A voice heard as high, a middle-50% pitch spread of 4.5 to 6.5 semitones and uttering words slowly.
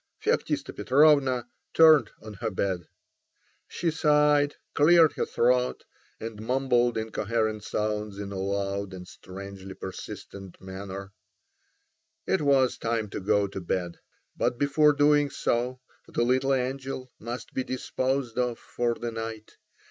No: low, 120 Hz; average, 5.1 semitones; slow, 130 wpm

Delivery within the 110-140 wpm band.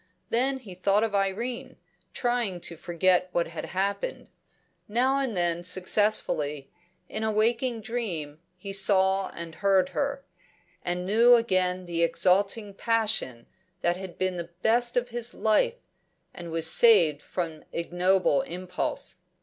Yes: slow, 135 wpm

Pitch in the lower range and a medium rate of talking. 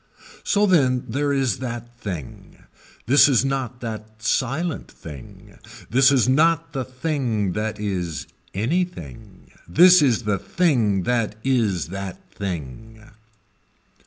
No: low, 120 Hz; slow, 120 wpm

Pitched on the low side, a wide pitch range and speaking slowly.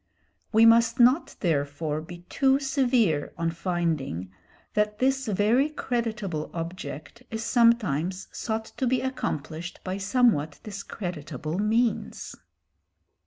No: high, 205 Hz; wide, 6.5 semitones; slow, 110 wpm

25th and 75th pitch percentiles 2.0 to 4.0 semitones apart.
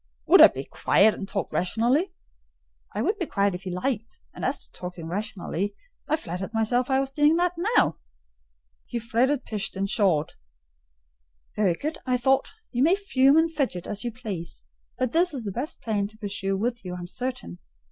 No: wide, 5.6 semitones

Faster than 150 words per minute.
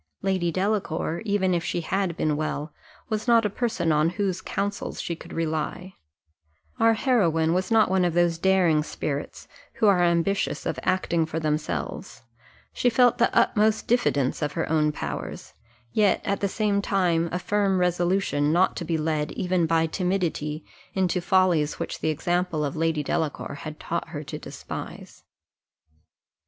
Yes: average, 160 wpm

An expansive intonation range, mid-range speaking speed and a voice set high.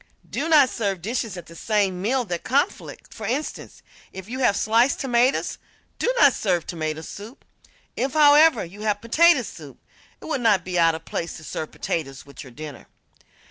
Yes: wide, 7.2 semitones; average, 180 wpm; high, 215 Hz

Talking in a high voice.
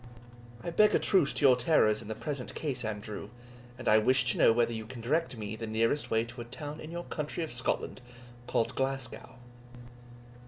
No: low, 125 Hz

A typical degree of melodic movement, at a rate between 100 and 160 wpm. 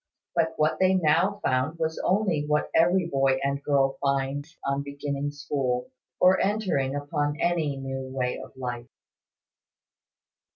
Yes: average, 3.5 semitones; slow, 135 wpm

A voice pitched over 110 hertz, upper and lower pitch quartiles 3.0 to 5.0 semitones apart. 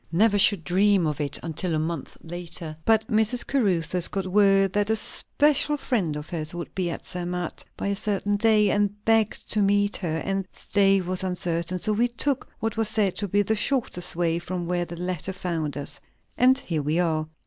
Yes: high, 190 Hz; average, 3.5 semitones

